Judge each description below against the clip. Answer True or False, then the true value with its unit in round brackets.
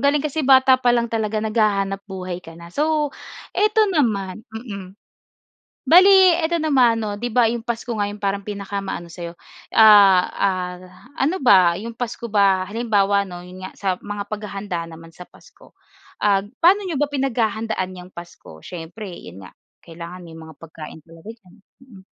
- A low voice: False (205 Hz)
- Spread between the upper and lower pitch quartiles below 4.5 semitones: False (4.8 semitones)